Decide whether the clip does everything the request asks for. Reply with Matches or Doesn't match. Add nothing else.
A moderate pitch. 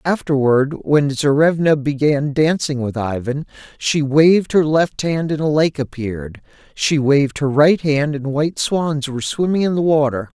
Matches